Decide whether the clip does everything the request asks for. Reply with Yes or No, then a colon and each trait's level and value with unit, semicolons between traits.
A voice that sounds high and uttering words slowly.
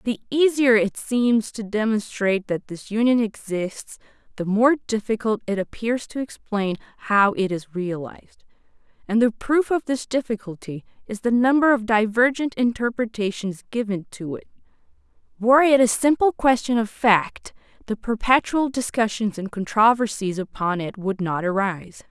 No: high, 220 Hz; average, 145 wpm